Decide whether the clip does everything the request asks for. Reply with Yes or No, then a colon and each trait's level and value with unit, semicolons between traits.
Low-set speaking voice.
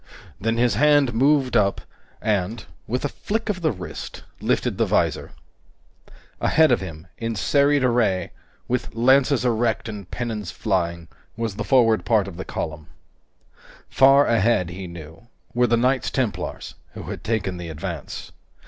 Yes: low, 115 Hz